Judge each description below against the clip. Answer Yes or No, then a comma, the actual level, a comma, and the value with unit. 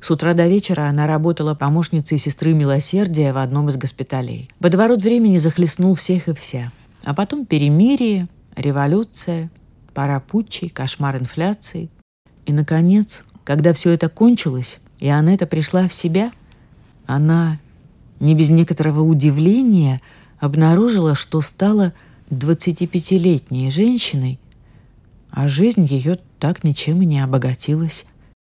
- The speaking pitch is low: No, medium, 160 Hz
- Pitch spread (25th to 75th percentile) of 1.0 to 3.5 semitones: No, average, 4.2 semitones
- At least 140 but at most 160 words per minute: No, average, 120 wpm